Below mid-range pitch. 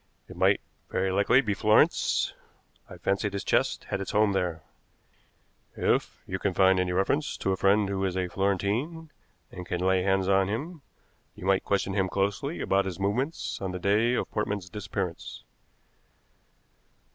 Yes: low, 100 Hz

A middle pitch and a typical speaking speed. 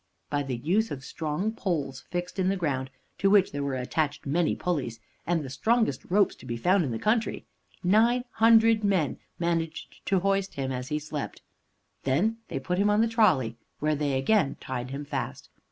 Yes: medium, 170 Hz; average, 185 wpm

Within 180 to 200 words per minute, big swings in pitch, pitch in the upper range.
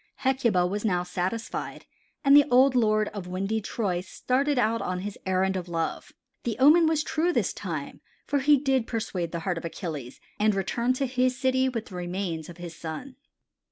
Yes: average, 190 wpm; wide, 6.4 semitones; high, 215 Hz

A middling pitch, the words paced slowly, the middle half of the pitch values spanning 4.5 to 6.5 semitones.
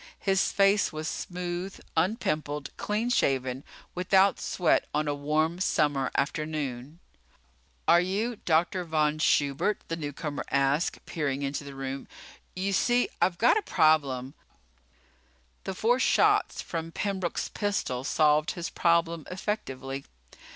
Yes: medium, 155 Hz; slow, 125 wpm; average, 4.8 semitones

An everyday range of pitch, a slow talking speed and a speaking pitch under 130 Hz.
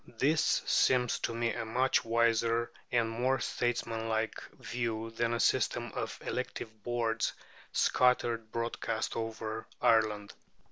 No: narrow, 1.2 semitones; slow, 120 wpm; low, 115 Hz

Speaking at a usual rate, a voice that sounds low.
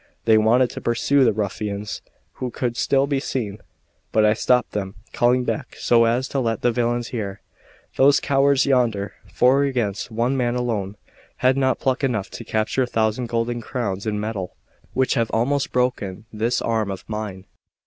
Yes: average, 175 wpm; low, 120 Hz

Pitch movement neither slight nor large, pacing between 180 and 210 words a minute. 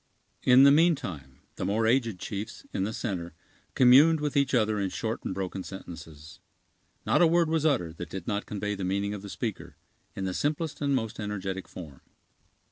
No: wide, 6.4 semitones; average, 190 wpm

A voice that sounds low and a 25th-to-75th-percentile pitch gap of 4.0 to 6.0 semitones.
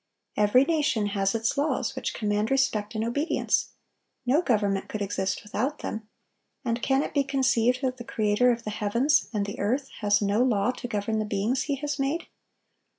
No: high, 230 Hz; average, 4.5 semitones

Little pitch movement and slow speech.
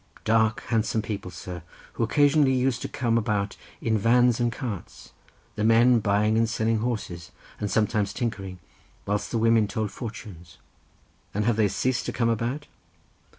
No: narrow, 2.3 semitones; average, 155 wpm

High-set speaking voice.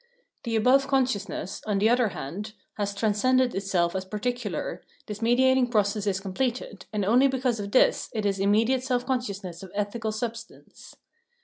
Yes: high, 220 Hz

